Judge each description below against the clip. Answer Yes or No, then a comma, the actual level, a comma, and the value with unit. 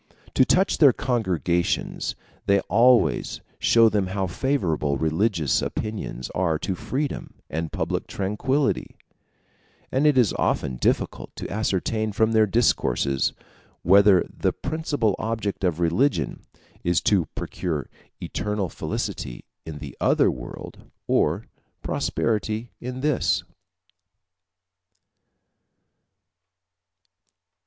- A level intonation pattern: No, wide, 5.6 semitones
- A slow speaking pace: Yes, slow, 100 wpm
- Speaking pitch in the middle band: No, low, 105 Hz